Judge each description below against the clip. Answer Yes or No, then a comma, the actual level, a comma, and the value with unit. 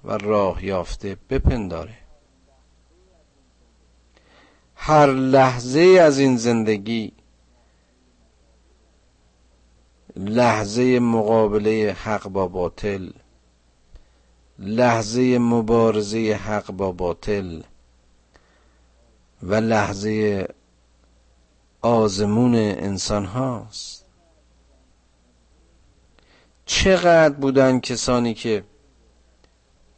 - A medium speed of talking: No, slow, 55 wpm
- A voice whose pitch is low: Yes, very low, 95 Hz